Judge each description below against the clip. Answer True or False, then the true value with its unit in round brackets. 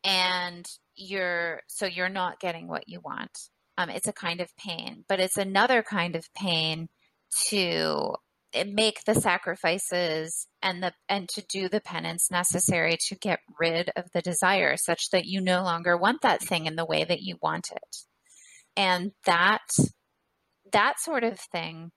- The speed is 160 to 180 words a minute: True (165 wpm)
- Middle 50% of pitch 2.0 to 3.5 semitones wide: True (2.7 semitones)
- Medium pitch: True (180 Hz)